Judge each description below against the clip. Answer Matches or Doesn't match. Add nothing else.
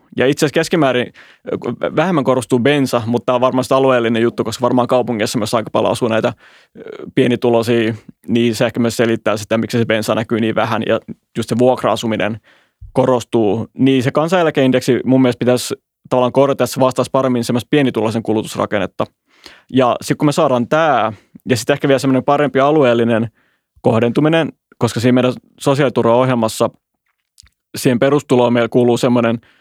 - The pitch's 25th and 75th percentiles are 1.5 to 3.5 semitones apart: Matches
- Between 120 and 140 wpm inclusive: Doesn't match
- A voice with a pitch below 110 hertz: Doesn't match